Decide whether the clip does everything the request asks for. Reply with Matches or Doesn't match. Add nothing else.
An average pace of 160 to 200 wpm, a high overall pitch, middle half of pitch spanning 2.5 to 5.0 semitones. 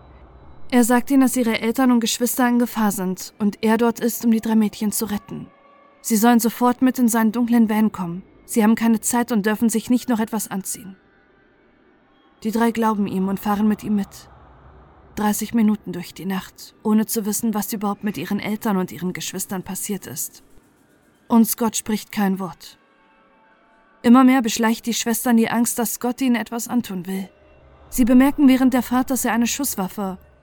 Matches